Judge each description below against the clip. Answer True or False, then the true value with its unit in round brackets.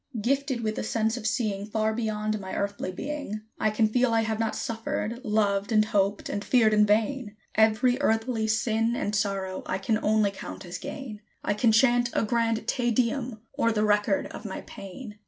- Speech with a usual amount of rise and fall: False (2.1 semitones)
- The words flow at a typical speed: True (190 wpm)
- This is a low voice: False (220 Hz)